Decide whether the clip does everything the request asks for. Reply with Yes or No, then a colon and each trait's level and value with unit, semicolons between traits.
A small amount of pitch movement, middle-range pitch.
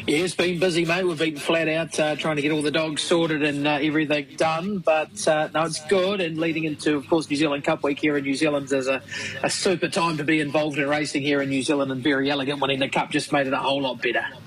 Yes: narrow, 2.1 semitones; medium, 155 Hz